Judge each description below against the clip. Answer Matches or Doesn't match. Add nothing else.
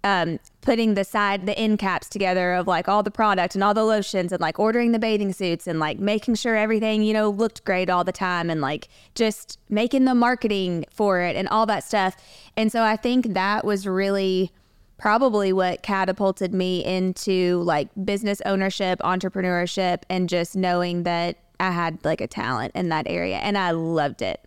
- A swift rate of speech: Doesn't match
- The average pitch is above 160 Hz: Matches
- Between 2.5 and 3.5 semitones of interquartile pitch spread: Matches